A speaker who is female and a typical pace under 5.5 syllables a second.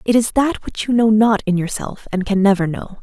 Yes: female; 5.3 syllables/s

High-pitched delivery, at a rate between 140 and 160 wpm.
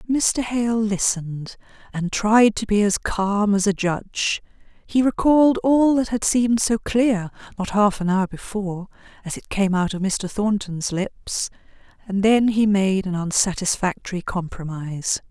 Yes: high, 205 Hz; average, 155 wpm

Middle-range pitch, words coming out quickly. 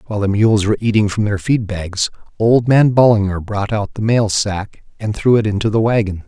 No: low, 105 Hz; fast, 220 wpm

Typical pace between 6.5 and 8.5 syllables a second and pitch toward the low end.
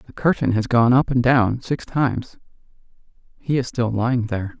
No: 5.1 syllables/s; low, 120 Hz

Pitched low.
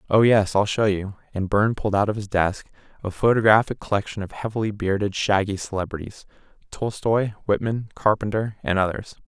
Yes: low, 105 Hz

